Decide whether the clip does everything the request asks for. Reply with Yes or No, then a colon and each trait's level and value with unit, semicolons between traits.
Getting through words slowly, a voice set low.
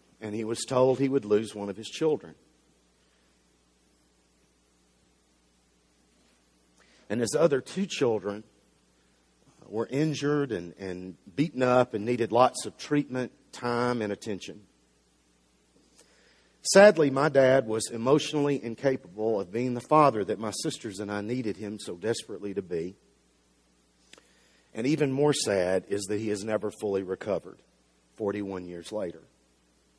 Yes: slow, 130 wpm; low, 100 Hz